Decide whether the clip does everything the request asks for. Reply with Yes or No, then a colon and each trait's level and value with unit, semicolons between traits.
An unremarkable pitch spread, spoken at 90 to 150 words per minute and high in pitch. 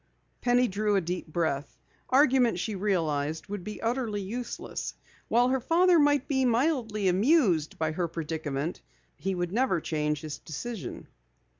No: wide, 7.3 semitones; average, 145 wpm; high, 200 Hz